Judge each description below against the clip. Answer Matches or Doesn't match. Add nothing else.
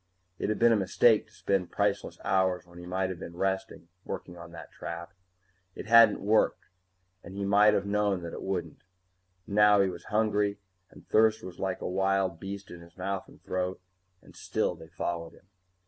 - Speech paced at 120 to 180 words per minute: Doesn't match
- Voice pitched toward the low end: Matches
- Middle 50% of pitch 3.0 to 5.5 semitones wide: Doesn't match